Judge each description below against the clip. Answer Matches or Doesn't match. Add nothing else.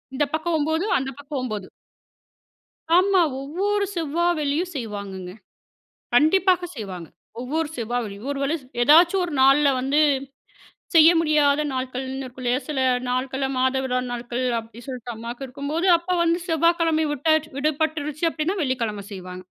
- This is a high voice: Matches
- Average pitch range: Matches